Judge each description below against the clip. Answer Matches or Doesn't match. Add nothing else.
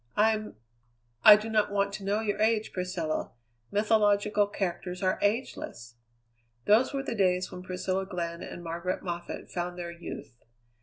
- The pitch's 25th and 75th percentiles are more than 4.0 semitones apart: Doesn't match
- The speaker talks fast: Doesn't match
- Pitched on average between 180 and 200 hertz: Matches